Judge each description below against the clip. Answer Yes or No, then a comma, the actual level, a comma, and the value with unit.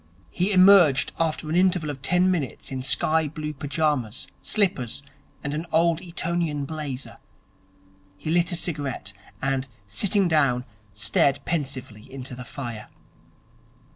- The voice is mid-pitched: Yes, medium, 150 Hz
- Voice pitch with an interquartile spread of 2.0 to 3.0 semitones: No, average, 4.5 semitones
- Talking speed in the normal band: No, slow, 130 wpm